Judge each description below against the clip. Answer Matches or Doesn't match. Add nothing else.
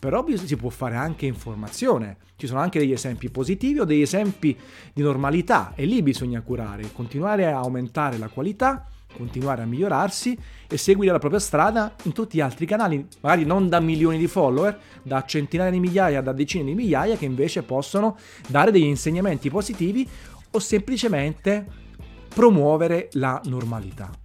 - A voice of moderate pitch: Matches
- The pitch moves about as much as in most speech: Doesn't match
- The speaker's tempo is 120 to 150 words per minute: Doesn't match